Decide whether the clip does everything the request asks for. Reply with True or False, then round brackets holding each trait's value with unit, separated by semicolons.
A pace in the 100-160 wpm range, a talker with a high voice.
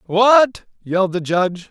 True (140 wpm; 200 Hz)